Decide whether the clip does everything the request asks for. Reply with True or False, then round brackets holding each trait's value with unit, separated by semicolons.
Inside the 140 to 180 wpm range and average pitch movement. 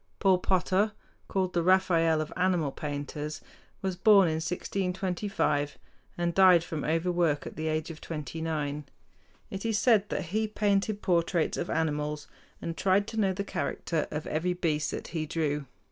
True (160 wpm; 3.5 semitones)